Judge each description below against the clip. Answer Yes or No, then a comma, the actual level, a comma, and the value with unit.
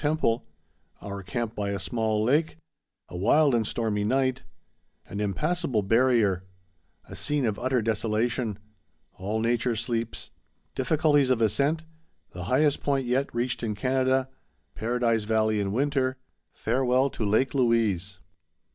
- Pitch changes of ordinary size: Yes, average, 4.1 semitones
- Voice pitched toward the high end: No, low, 115 Hz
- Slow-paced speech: Yes, slow, 100 wpm